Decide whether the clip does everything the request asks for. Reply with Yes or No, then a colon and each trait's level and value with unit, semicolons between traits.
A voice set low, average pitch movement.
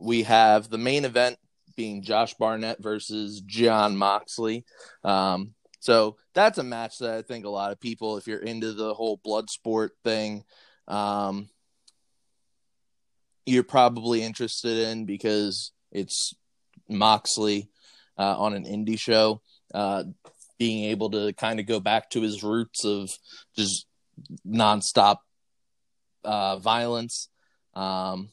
No: low, 110 Hz; narrow, 1.8 semitones